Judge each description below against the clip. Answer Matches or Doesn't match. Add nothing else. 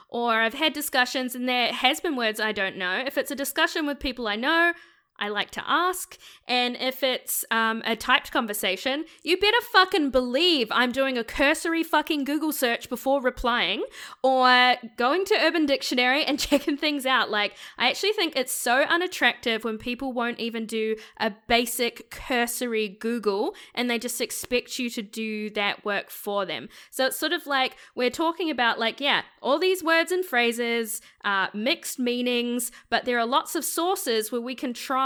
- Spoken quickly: Doesn't match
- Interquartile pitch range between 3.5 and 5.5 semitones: Matches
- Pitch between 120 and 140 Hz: Doesn't match